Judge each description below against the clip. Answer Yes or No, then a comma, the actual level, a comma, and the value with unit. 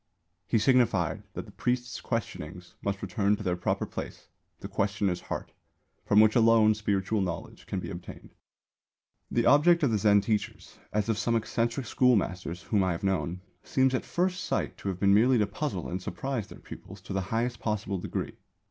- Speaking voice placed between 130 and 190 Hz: No, low, 105 Hz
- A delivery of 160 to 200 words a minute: Yes, average, 185 wpm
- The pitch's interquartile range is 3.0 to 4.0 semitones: Yes, average, 3.5 semitones